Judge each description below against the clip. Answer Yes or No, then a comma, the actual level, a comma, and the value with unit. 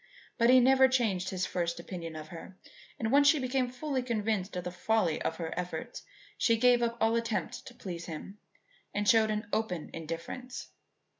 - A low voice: No, high, 220 Hz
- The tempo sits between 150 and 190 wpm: Yes, average, 180 wpm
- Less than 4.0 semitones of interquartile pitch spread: No, wide, 5.6 semitones